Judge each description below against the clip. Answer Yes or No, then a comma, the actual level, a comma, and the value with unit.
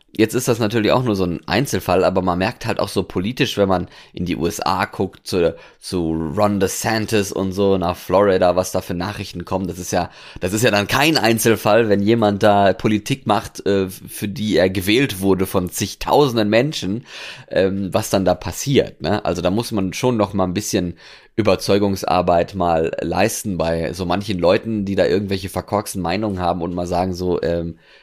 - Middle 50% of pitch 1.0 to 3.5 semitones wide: Yes, average, 2.9 semitones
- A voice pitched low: Yes, low, 100 Hz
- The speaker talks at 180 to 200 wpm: Yes, fast, 190 wpm